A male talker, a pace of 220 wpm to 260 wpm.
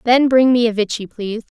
No: female; fast, 230 wpm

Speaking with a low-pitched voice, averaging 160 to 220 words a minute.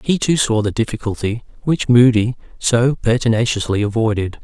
No: low, 115 Hz; slow, 135 wpm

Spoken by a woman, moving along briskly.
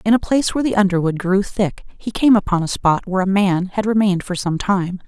Yes: female; fast, 250 wpm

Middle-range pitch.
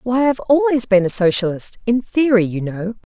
No: high, 215 Hz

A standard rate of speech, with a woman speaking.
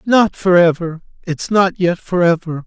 No: average, 180 wpm; male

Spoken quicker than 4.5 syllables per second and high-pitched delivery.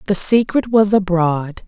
No: 4.0 syllables/s; high, 195 Hz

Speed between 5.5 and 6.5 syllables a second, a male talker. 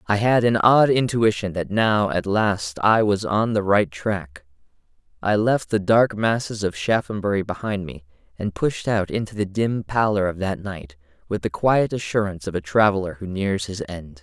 No: 4.7 syllables/s; male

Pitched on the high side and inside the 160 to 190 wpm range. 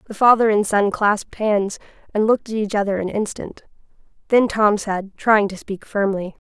Yes: high, 205 Hz; average, 185 wpm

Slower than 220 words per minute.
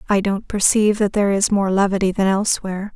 Yes: fast, 205 wpm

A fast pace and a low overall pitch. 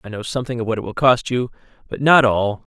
Yes: fast, 260 wpm; low, 120 Hz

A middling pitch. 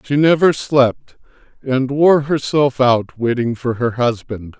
No: low, 130 Hz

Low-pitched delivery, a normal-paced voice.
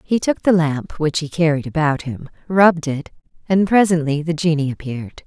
No: medium, 160 Hz; average, 180 wpm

